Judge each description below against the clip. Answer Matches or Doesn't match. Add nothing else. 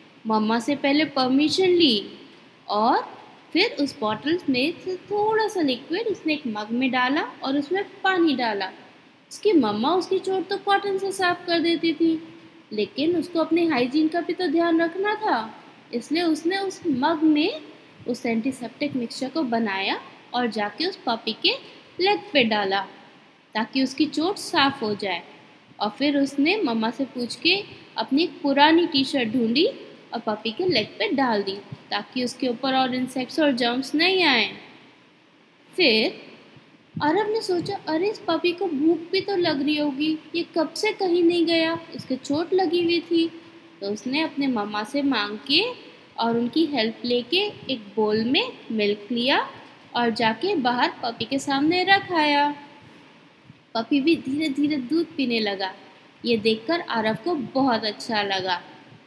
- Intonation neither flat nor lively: Doesn't match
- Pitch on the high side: Matches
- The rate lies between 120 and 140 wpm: Doesn't match